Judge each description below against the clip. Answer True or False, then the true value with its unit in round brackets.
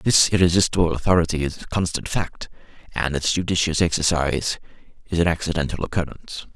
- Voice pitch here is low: True (80 Hz)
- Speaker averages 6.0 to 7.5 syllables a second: True (6.1 syllables/s)